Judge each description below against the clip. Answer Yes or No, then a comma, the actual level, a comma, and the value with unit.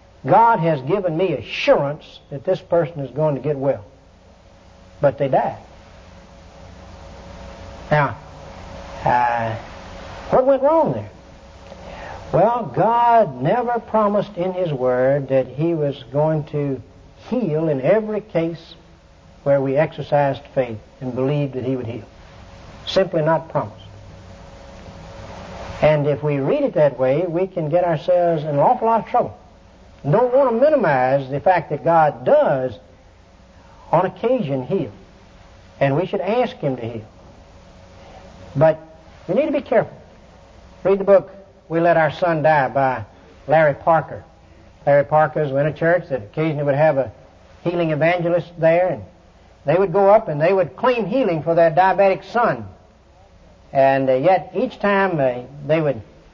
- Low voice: No, medium, 145 Hz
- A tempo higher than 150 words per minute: No, average, 145 wpm